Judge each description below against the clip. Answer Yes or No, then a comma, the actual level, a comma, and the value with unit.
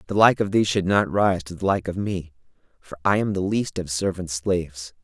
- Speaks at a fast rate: Yes, fast, 240 wpm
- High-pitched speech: No, very low, 95 Hz